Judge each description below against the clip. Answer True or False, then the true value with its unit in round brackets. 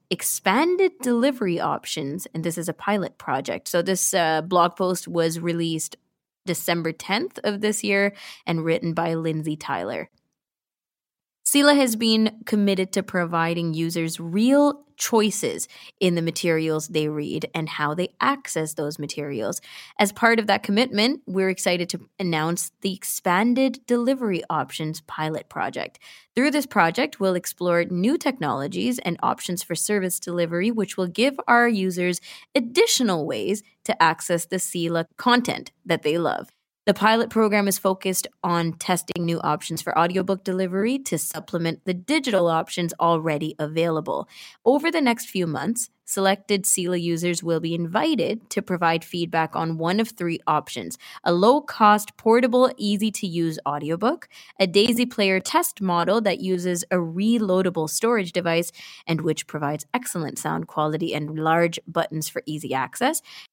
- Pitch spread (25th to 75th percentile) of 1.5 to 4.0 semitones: False (4.8 semitones)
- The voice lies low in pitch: False (185 Hz)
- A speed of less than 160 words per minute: True (150 wpm)